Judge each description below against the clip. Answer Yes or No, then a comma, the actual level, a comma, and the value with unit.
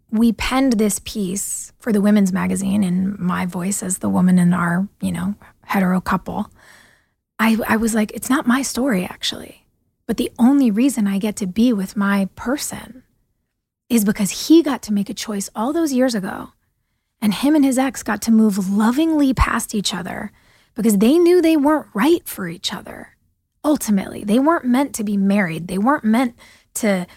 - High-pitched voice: Yes, high, 215 Hz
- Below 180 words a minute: No, average, 185 wpm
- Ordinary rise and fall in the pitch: Yes, average, 4.6 semitones